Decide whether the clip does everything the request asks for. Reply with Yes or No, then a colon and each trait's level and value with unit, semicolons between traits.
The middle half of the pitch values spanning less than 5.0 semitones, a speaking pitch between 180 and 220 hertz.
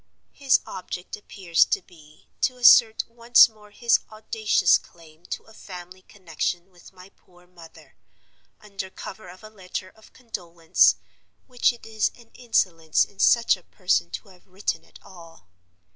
Yes: average, 3.9 semitones; medium, 185 Hz